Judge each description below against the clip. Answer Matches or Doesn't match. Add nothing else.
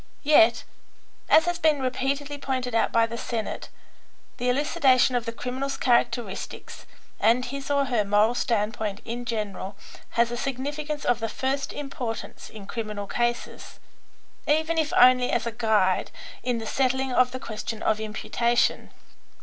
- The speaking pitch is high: Matches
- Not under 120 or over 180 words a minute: Matches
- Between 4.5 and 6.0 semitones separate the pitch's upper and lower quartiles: Doesn't match